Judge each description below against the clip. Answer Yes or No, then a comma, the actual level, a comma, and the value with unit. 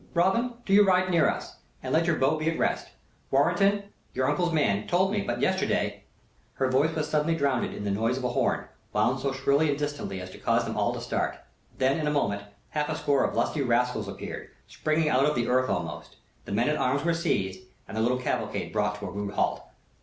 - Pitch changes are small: No, wide, 5.5 semitones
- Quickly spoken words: Yes, fast, 235 wpm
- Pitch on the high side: No, medium, 140 Hz